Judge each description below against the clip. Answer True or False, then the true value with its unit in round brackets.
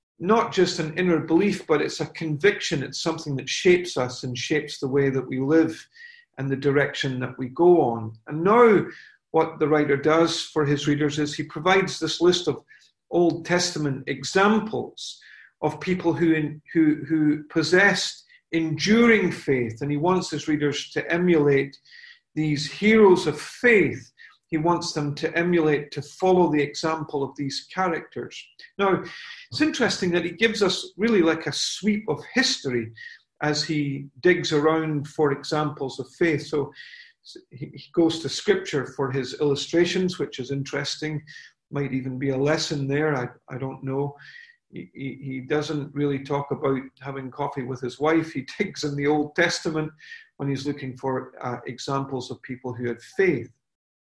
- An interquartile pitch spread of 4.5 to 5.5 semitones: False (4.0 semitones)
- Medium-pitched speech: True (150 Hz)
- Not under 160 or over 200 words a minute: True (165 wpm)